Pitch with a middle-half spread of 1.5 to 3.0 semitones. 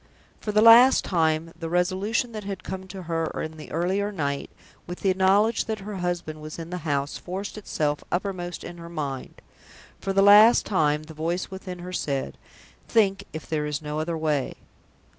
No: average, 3.9 semitones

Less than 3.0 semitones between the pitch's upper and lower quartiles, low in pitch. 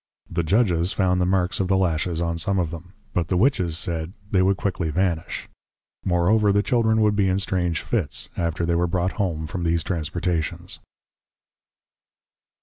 Yes: narrow, 2.5 semitones; very low, 90 Hz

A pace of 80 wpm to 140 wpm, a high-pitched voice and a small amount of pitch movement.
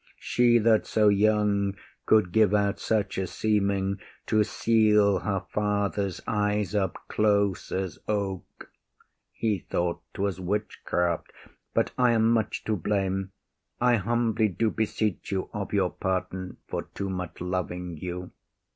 No: slow, 135 wpm; low, 100 Hz; narrow, 2.3 semitones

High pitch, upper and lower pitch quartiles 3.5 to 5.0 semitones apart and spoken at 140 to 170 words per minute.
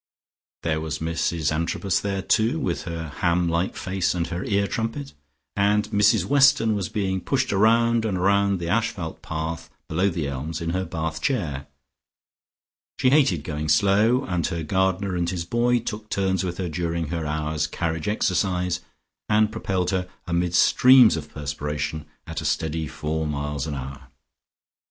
No: very low, 90 Hz; average, 4.4 semitones; average, 160 wpm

